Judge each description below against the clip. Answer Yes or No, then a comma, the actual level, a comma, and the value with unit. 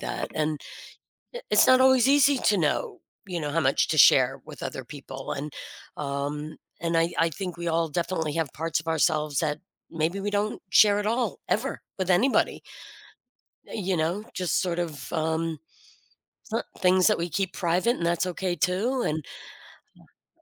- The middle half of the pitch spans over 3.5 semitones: Yes, average, 4.2 semitones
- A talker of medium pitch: Yes, medium, 170 Hz